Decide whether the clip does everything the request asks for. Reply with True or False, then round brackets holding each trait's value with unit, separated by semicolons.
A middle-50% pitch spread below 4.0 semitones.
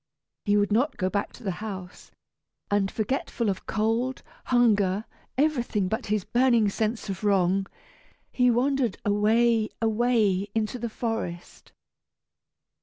True (3.0 semitones)